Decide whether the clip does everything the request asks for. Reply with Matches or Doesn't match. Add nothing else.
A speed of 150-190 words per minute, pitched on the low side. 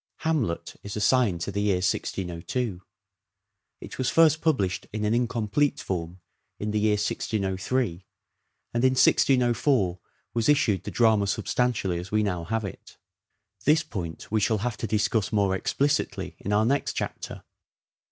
Matches